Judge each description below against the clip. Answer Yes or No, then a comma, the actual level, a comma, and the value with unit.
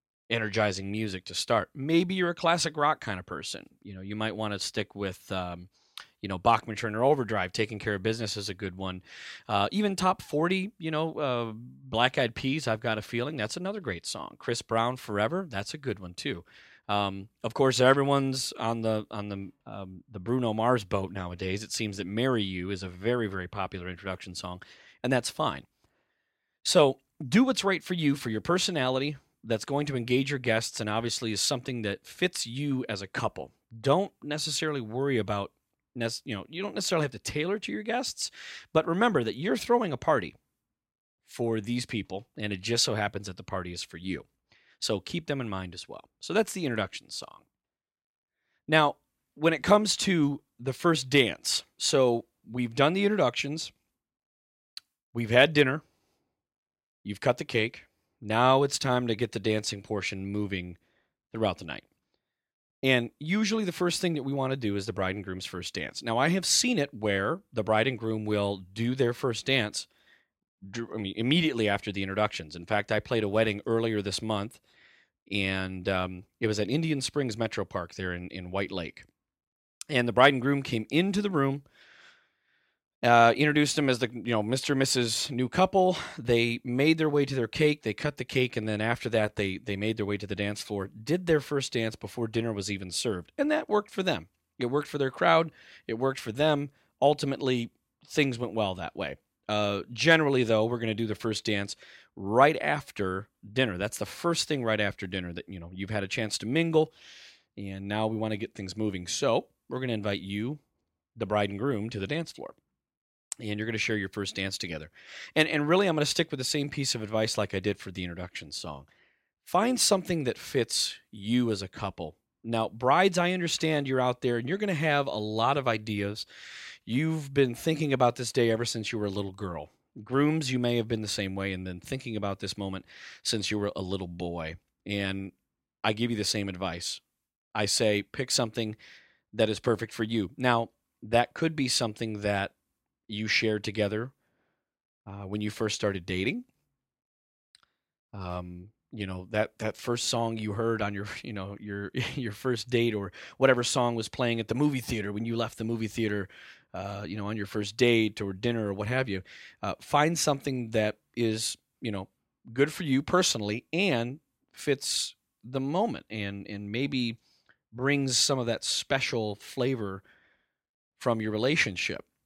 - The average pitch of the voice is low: Yes, low, 115 Hz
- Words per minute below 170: No, average, 200 wpm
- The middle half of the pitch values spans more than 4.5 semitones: Yes, average, 5.1 semitones